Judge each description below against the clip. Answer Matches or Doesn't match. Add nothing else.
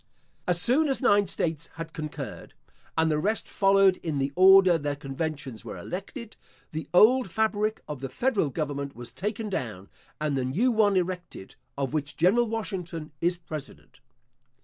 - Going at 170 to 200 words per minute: Doesn't match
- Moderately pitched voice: Matches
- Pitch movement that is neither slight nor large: Doesn't match